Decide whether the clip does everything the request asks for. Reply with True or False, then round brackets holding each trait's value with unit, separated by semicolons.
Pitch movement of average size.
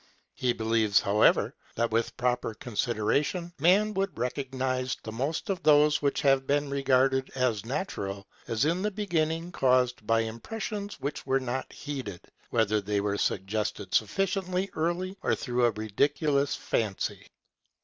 False (5.9 semitones)